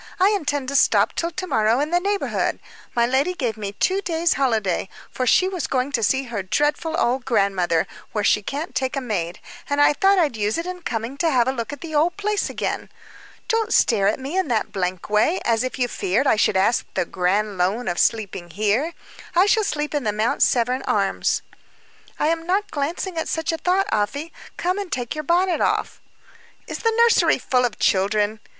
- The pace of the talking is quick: Yes, fast, 210 wpm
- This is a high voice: Yes, very high, 260 Hz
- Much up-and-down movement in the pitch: Yes, wide, 7.9 semitones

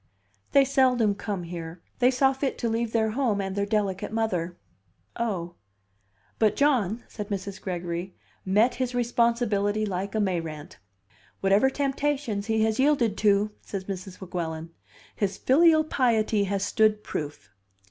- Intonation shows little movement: No, average, 4.2 semitones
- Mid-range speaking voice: No, high, 210 Hz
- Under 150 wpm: Yes, average, 140 wpm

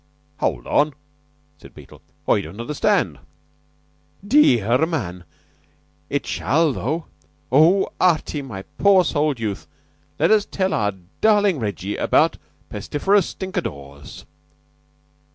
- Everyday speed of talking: No, slow, 105 wpm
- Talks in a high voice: No, medium, 150 Hz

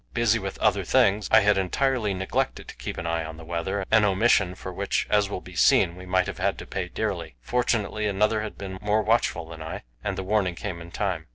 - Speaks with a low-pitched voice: Yes, very low, 95 Hz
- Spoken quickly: Yes, fast, 235 wpm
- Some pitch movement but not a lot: Yes, average, 3.3 semitones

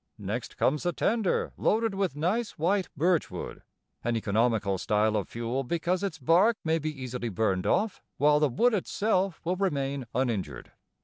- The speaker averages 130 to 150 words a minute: No, average, 165 wpm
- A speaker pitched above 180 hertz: No, medium, 150 Hz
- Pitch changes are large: Yes, wide, 7.8 semitones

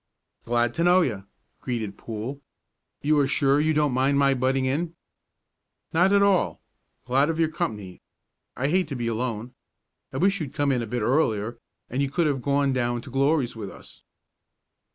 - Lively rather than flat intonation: No, average, 4.3 semitones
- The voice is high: No, low, 135 Hz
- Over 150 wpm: Yes, average, 180 wpm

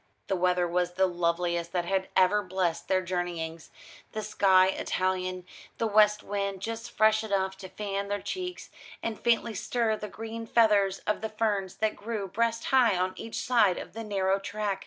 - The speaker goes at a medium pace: Yes, average, 180 wpm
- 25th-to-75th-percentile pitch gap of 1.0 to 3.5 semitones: Yes, average, 2.9 semitones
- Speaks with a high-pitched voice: Yes, high, 195 Hz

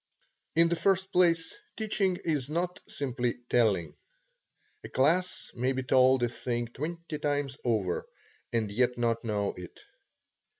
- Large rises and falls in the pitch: Yes, wide, 5.9 semitones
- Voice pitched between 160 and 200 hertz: No, low, 130 Hz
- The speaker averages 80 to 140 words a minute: Yes, slow, 135 wpm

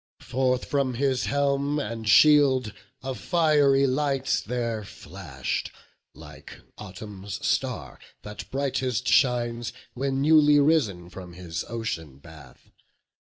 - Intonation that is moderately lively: No, wide, 5.9 semitones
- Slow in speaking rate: Yes, slow, 110 wpm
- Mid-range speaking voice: No, low, 125 Hz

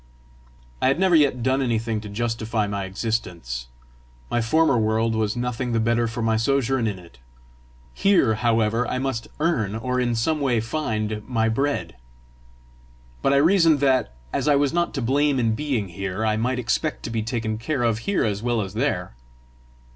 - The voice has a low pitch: Yes, low, 115 Hz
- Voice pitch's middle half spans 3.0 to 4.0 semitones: Yes, average, 3.6 semitones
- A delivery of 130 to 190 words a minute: Yes, average, 180 wpm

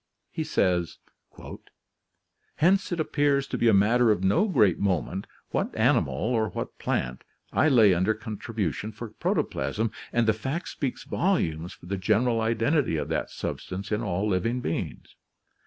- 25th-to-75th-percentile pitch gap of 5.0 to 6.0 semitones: No, average, 4.6 semitones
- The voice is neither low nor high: No, low, 110 Hz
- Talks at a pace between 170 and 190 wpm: No, average, 155 wpm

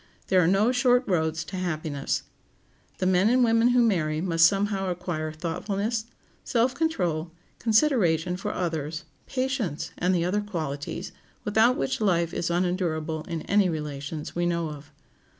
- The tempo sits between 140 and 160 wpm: Yes, average, 150 wpm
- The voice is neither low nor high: Yes, medium, 180 Hz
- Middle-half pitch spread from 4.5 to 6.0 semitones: Yes, average, 4.9 semitones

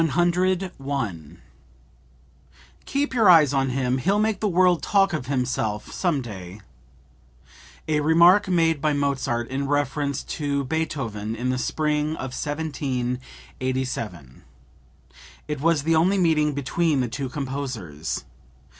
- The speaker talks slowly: Yes, slow, 120 wpm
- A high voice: No, medium, 145 Hz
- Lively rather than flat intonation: No, average, 4.3 semitones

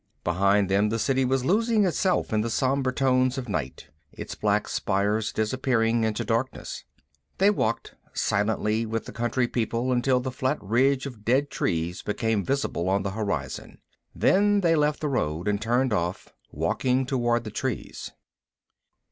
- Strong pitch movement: No, average, 4.1 semitones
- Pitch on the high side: No, low, 120 Hz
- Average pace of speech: Yes, average, 155 wpm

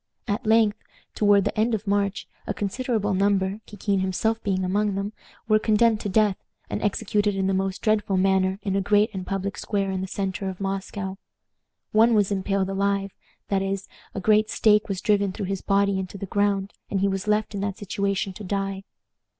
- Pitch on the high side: Yes, high, 200 Hz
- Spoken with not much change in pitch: Yes, narrow, 1.4 semitones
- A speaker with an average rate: Yes, average, 190 wpm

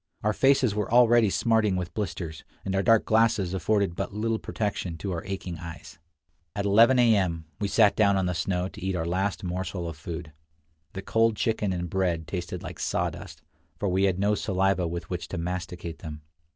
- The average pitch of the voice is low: Yes, very low, 95 Hz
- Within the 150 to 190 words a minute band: No, fast, 205 wpm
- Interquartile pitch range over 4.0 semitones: No, average, 3.3 semitones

